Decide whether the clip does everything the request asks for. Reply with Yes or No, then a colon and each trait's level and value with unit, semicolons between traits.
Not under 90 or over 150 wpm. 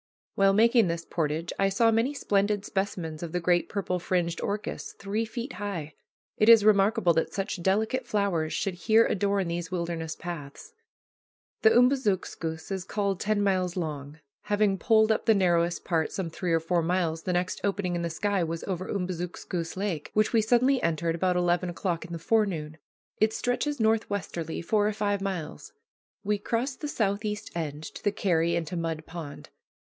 No: average, 175 wpm